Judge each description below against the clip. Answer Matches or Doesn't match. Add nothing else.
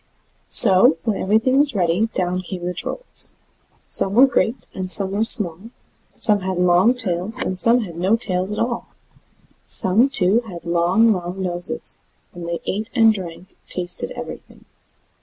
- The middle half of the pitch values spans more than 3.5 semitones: Matches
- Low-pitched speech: Doesn't match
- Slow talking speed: Doesn't match